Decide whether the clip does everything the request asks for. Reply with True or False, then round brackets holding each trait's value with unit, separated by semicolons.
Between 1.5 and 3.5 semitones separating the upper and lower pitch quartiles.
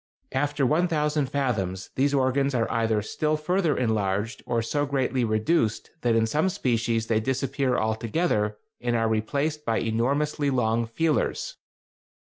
False (4.6 semitones)